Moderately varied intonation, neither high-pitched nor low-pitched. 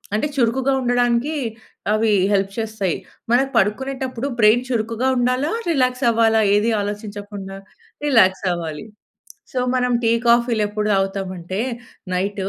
No: average, 3.6 semitones; high, 225 Hz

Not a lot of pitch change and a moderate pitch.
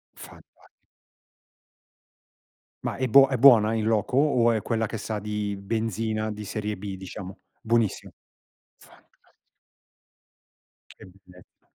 No: narrow, 2.0 semitones; low, 110 Hz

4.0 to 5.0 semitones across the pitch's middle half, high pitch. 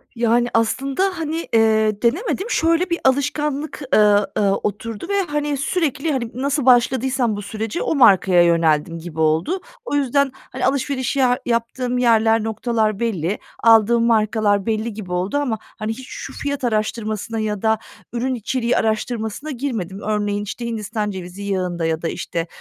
Yes: average, 4.3 semitones; high, 230 Hz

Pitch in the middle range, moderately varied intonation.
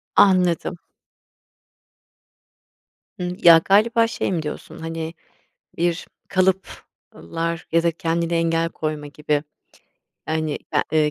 No: medium, 165 Hz; narrow, 2.1 semitones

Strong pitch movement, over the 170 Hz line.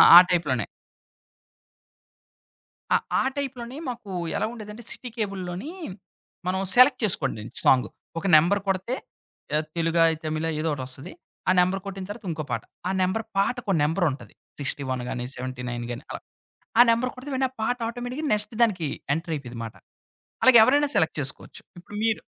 Yes: wide, 8.0 semitones; medium, 185 Hz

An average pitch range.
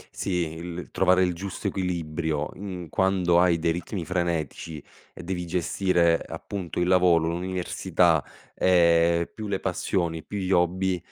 No: narrow, 1.8 semitones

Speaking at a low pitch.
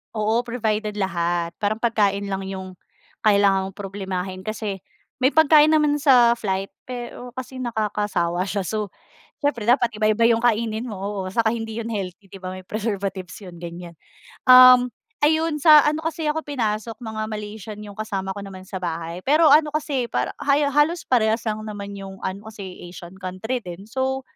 No: high, 215 Hz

